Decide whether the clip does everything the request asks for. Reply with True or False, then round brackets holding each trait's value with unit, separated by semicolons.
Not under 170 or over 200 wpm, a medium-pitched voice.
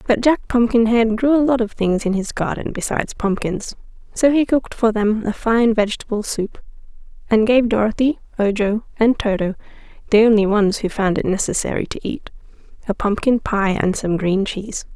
False (175 wpm; 220 Hz)